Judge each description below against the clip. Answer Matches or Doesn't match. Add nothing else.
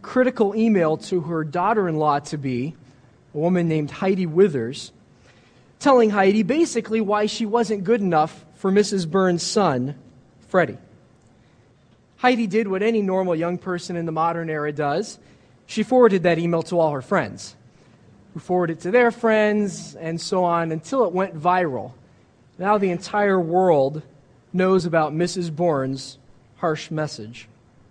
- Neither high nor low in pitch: Matches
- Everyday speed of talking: Matches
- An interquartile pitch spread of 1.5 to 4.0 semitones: Doesn't match